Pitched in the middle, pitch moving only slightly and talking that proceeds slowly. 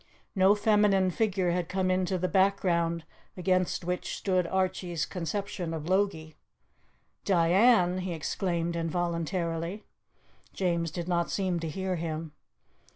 Yes: medium, 180 Hz; narrow, 2.1 semitones; slow, 120 wpm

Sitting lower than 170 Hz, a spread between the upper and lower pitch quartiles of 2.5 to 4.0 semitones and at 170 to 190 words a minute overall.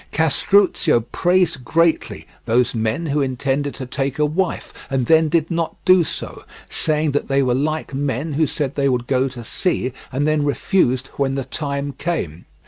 Yes: medium, 140 Hz; average, 3.4 semitones; average, 175 wpm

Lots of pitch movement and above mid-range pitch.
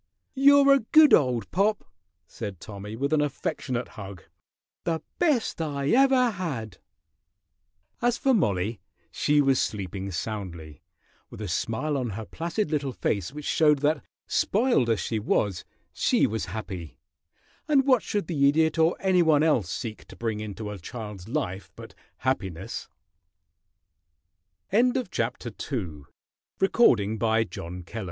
No: wide, 8.3 semitones; low, 135 Hz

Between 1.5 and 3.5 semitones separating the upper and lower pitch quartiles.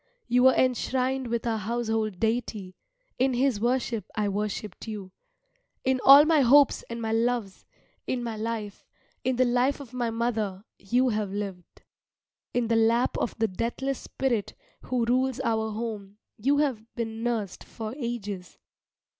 Yes: average, 2.8 semitones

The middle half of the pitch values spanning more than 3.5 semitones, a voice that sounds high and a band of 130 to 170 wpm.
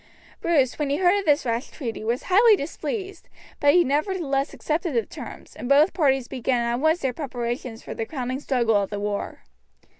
No: average, 5.0 semitones; very high, 275 Hz; average, 190 wpm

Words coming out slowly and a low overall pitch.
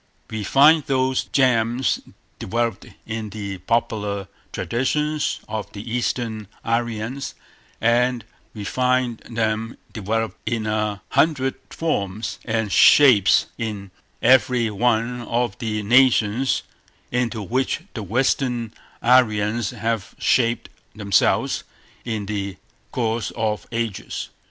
Yes: slow, 105 wpm; low, 115 Hz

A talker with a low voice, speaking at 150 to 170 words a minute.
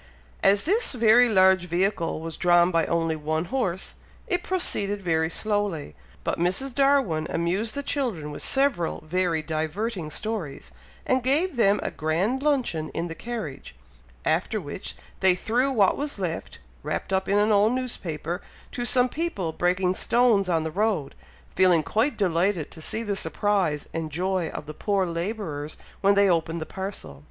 No: high, 190 Hz; average, 165 wpm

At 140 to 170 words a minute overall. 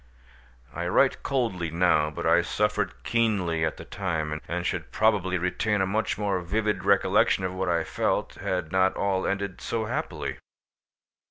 Yes: average, 160 wpm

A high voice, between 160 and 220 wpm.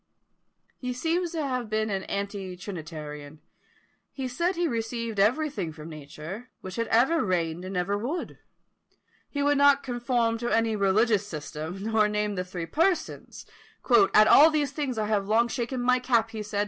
Yes: high, 220 Hz; average, 170 wpm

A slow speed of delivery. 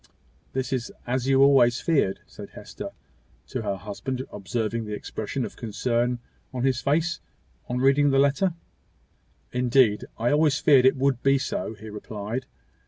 No: average, 155 wpm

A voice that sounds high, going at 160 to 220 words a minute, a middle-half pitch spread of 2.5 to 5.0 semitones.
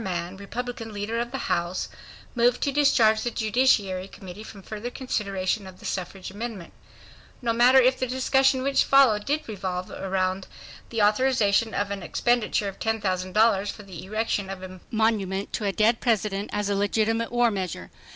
Yes: high, 215 Hz; average, 170 wpm; average, 3.7 semitones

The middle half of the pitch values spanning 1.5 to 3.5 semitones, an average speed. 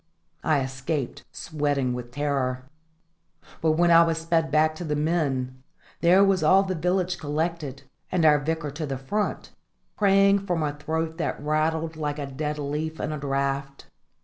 Yes: average, 2.9 semitones; average, 165 wpm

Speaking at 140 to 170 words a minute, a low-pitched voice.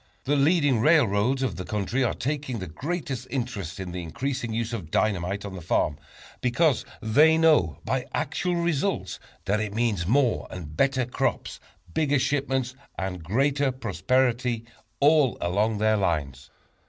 Yes: average, 150 wpm; low, 120 Hz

